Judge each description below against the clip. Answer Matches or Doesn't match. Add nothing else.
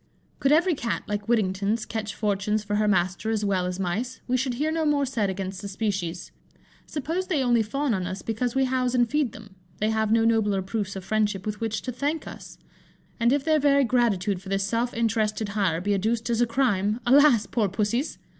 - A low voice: Doesn't match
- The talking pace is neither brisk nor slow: Doesn't match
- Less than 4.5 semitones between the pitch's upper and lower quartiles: Matches